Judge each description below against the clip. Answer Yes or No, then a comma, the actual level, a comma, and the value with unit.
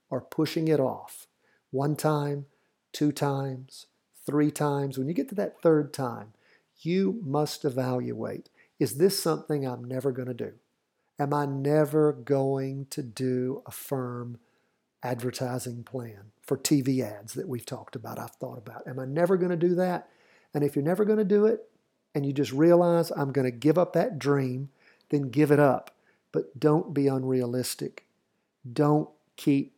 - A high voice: No, medium, 140 Hz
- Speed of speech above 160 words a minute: Yes, average, 170 wpm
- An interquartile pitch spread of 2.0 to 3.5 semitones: Yes, average, 2.8 semitones